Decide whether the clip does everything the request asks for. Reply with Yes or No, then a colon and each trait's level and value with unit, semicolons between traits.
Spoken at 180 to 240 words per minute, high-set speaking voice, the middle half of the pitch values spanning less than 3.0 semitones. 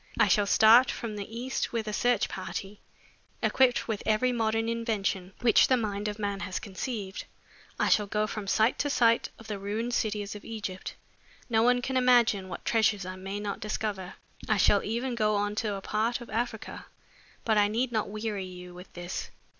Yes: average, 195 wpm; high, 215 Hz; narrow, 2.5 semitones